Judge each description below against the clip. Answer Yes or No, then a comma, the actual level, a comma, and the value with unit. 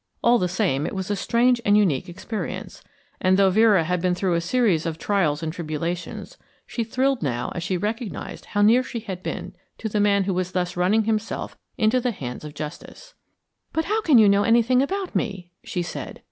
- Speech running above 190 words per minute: Yes, fast, 205 wpm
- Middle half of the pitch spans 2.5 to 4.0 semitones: No, average, 4.6 semitones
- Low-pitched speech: No, high, 200 Hz